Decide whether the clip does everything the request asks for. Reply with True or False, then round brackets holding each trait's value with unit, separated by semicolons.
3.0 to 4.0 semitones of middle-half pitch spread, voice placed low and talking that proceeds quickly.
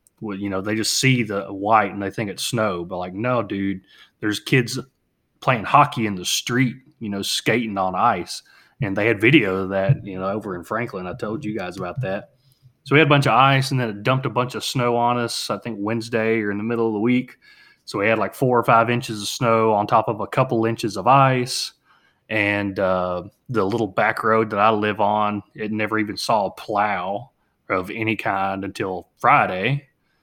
True (3.6 semitones; 110 Hz; 220 wpm)